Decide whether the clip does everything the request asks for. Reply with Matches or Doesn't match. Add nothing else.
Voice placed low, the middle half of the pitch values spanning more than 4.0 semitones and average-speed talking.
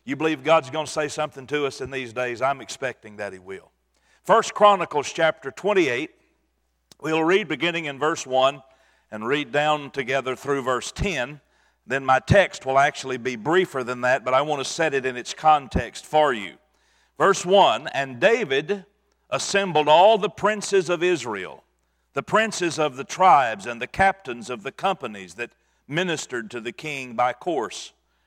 Doesn't match